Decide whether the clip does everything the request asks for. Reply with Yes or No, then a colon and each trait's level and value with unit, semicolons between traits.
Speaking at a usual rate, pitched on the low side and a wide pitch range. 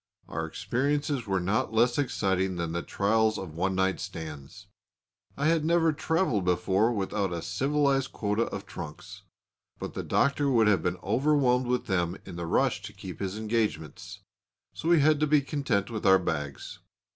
Yes: average, 170 wpm; low, 110 Hz; wide, 6.8 semitones